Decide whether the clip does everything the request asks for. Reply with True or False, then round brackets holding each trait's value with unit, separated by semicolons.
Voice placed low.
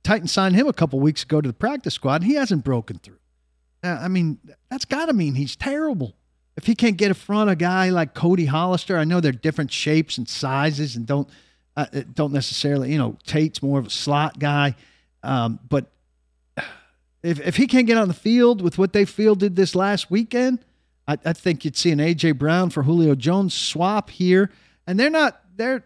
False (160 Hz)